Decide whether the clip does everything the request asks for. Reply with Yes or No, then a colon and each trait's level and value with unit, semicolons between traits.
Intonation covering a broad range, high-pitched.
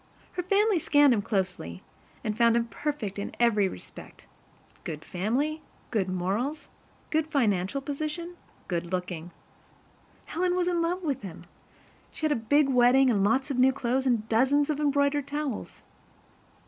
Yes: wide, 6.4 semitones; very high, 260 Hz